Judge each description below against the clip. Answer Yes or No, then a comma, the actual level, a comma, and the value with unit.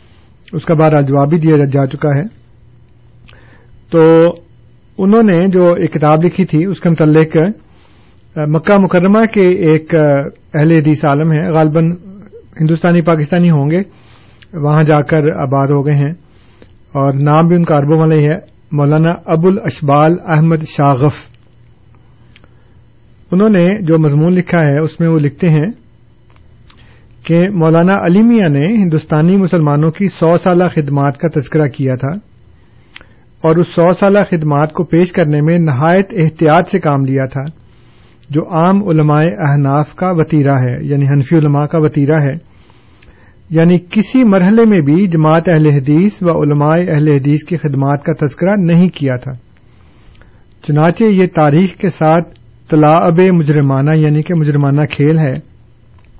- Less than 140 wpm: No, average, 145 wpm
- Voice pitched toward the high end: No, medium, 155 Hz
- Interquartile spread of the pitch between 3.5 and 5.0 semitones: Yes, average, 3.9 semitones